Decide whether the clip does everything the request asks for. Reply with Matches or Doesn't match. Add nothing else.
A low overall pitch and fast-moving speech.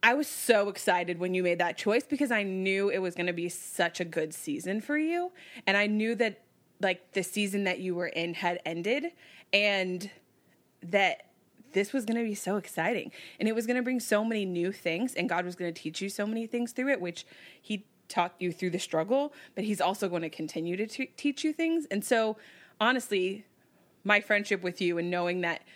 Doesn't match